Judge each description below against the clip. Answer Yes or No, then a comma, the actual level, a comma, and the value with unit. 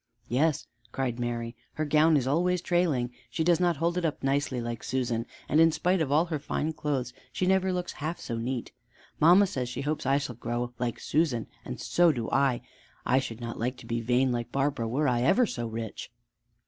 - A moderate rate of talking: No, fast, 210 wpm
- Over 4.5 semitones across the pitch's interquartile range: Yes, average, 5.0 semitones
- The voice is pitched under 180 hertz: Yes, low, 135 Hz